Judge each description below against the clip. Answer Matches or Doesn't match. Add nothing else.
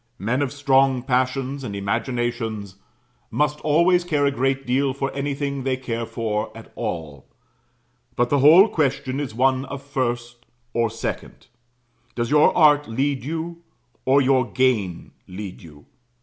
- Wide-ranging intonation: Doesn't match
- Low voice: Matches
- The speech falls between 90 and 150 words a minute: Matches